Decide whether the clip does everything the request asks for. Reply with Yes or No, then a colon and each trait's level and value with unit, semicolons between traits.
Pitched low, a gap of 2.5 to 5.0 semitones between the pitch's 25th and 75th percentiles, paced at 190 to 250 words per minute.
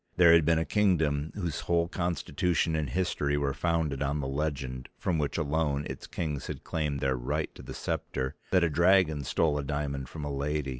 Yes: very low, 75 Hz; average, 2.8 semitones; average, 200 wpm